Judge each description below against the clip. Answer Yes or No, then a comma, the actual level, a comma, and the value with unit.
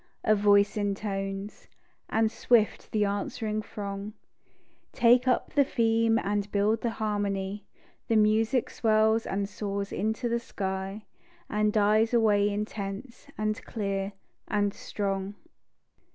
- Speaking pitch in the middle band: No, high, 210 Hz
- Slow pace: Yes, slow, 120 wpm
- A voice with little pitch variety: Yes, narrow, 1.7 semitones